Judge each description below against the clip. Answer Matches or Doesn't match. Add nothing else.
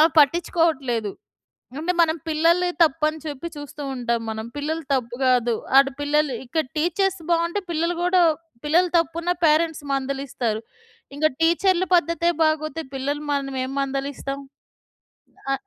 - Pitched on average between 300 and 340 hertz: Matches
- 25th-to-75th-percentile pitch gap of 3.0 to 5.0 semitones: Matches